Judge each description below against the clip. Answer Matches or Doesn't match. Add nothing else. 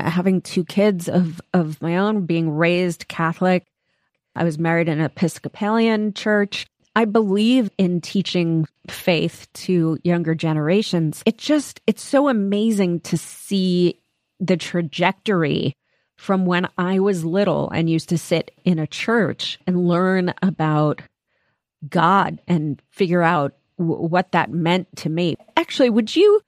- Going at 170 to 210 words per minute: Doesn't match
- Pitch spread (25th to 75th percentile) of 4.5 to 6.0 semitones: Doesn't match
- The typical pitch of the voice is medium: Matches